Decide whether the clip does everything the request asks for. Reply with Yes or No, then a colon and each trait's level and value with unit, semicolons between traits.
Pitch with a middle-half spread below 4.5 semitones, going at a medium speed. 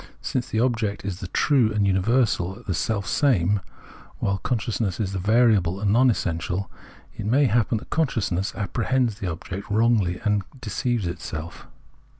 Yes: average, 3.8 semitones; average, 155 wpm